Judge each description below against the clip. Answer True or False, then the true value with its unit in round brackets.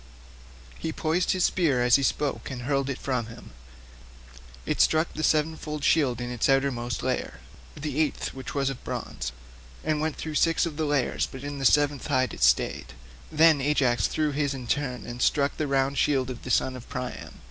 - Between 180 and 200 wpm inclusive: True (190 wpm)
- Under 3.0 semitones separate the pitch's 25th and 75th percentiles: False (3.4 semitones)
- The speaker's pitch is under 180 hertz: True (135 Hz)